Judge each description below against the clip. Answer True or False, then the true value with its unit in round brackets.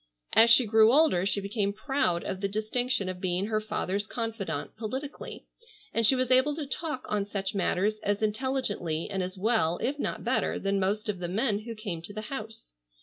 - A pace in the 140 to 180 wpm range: False (200 wpm)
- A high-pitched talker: True (215 Hz)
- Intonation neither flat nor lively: True (3.5 semitones)